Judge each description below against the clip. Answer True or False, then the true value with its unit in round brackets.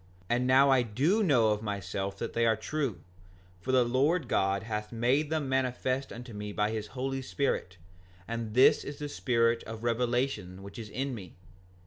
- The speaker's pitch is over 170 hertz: False (120 Hz)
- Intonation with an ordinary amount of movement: True (3.9 semitones)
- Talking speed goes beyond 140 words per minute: True (180 wpm)